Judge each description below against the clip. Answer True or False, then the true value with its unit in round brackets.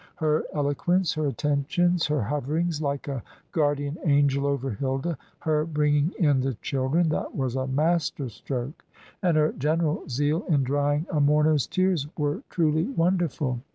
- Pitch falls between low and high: True (150 Hz)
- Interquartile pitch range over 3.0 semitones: False (2.5 semitones)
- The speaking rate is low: False (150 wpm)